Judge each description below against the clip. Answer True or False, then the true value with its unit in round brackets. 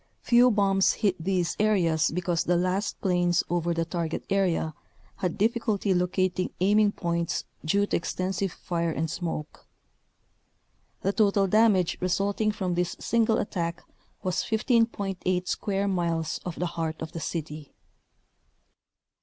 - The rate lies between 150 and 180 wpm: False (140 wpm)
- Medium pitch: True (180 Hz)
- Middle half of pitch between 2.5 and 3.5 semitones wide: True (2.9 semitones)